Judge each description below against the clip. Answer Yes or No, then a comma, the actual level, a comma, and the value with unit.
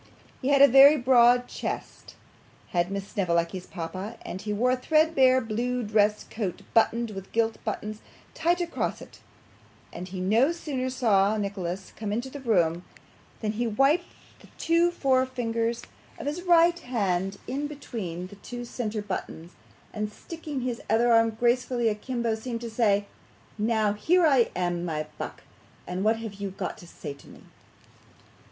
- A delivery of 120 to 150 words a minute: No, average, 160 wpm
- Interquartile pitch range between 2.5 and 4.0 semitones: No, average, 4.5 semitones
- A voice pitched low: No, high, 225 Hz